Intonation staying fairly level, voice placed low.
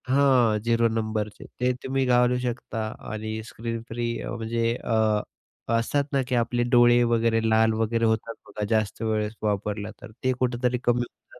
Yes: narrow, 1.7 semitones; low, 115 Hz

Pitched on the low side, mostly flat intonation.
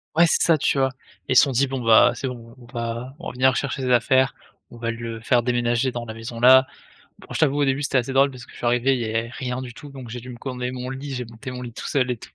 Yes: low, 125 Hz; narrow, 1.9 semitones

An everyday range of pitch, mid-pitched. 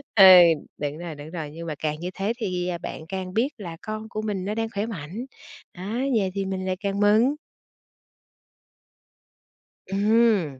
No: average, 4.1 semitones; high, 195 Hz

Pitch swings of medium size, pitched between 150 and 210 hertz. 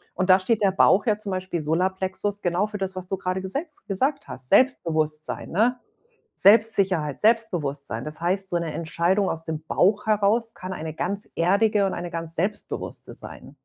Yes: average, 3.7 semitones; high, 190 Hz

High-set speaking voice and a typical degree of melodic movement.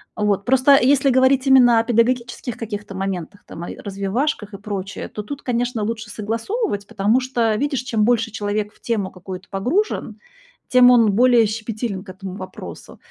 Yes: high, 225 Hz; average, 3.6 semitones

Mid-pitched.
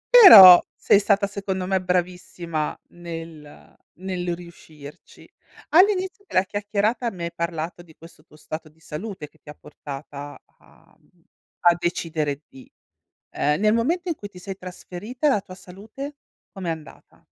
Yes: medium, 180 Hz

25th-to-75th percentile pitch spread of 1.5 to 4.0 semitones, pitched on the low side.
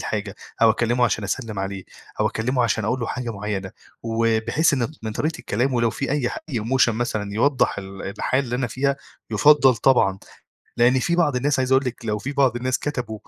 Yes: average, 3.5 semitones; low, 120 Hz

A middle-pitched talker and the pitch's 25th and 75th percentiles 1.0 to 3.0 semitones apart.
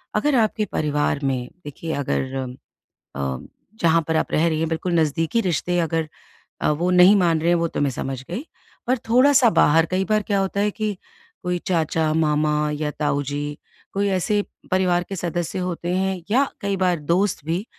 No: medium, 170 Hz; average, 3.9 semitones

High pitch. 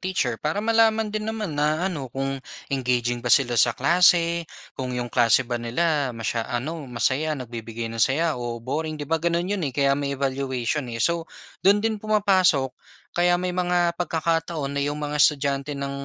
No: medium, 145 Hz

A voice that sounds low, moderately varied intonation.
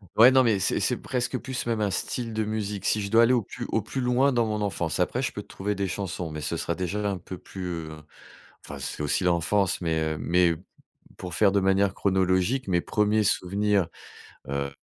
Yes: low, 100 Hz; average, 3.6 semitones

